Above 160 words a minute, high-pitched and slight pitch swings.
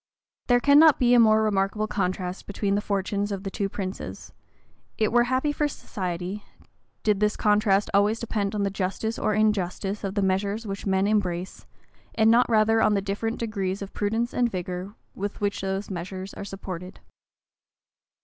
Yes: average, 170 wpm; high, 205 Hz; narrow, 2.1 semitones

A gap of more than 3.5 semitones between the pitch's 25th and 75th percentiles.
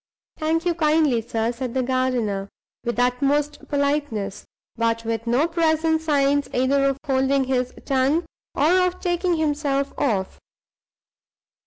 Yes: average, 4.0 semitones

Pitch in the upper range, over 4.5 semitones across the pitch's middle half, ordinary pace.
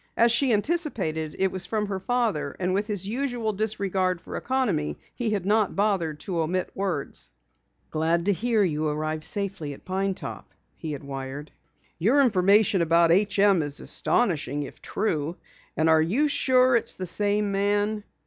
Yes: high, 195 Hz; average, 5.0 semitones; average, 170 wpm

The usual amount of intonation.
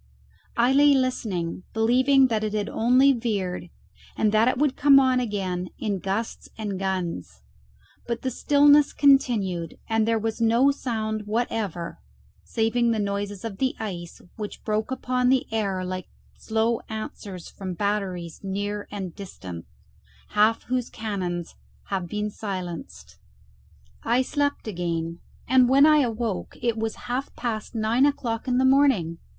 Yes: average, 4.5 semitones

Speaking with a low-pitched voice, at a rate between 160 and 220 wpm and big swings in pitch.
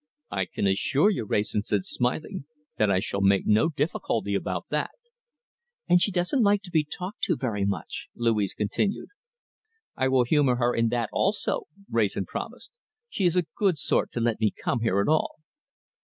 Yes: low, 120 Hz; average, 180 wpm; wide, 8.7 semitones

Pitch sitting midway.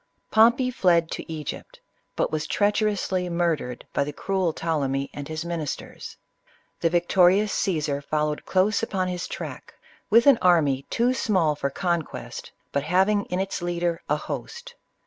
Yes: medium, 175 Hz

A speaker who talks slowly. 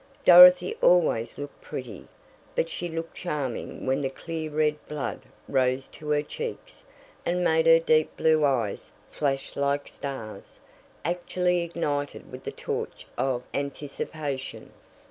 Yes: slow, 130 wpm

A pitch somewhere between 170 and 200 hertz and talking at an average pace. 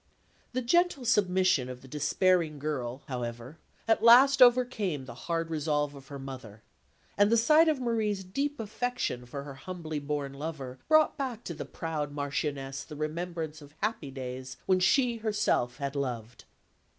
No: medium, 155 Hz; average, 160 wpm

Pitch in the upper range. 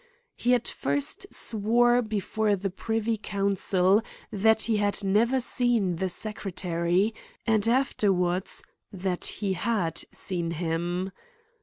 Yes: high, 200 Hz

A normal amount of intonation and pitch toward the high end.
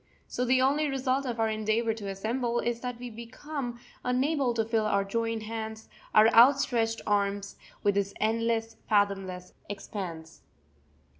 Yes: average, 3.1 semitones; high, 225 Hz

